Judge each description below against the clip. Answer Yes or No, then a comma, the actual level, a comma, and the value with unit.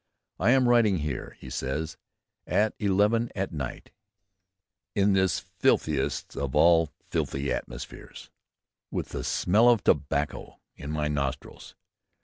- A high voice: No, very low, 80 Hz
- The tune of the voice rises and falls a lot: Yes, wide, 6.3 semitones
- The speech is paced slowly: Yes, slow, 125 wpm